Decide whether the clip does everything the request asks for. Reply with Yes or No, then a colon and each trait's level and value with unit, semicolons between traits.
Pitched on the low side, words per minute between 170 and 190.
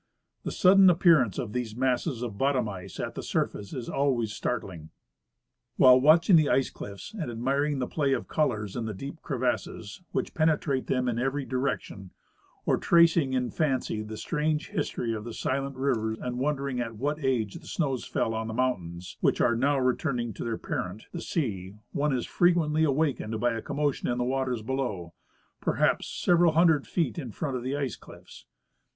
Yes: low, 130 Hz; average, 185 wpm